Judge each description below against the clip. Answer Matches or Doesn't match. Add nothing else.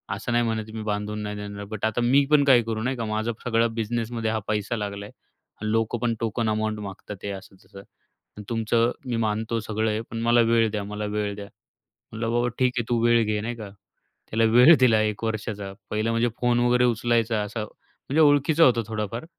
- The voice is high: Doesn't match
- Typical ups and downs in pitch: Doesn't match